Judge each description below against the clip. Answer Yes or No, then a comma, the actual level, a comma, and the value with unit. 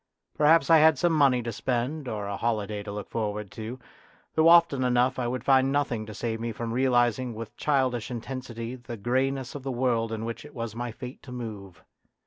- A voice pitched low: Yes, low, 120 Hz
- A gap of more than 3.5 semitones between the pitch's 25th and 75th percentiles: No, average, 2.8 semitones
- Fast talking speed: Yes, fast, 210 wpm